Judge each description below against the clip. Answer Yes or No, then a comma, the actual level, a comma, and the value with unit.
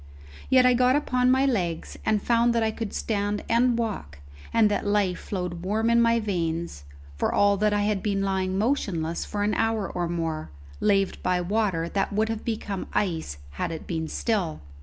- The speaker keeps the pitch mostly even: No, average, 4.1 semitones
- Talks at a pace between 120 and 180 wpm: No, average, 190 wpm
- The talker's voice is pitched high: Yes, high, 205 Hz